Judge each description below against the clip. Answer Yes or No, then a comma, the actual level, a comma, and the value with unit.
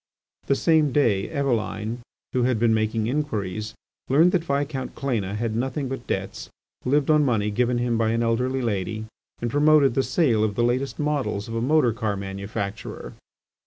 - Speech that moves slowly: No, average, 170 wpm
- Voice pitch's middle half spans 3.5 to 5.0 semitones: Yes, average, 4.2 semitones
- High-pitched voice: No, low, 120 Hz